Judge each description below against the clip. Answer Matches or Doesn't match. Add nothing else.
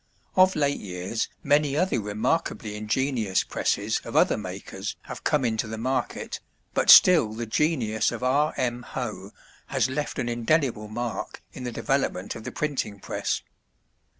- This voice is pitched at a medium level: Doesn't match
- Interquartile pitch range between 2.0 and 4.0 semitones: Doesn't match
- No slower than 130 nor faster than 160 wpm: Matches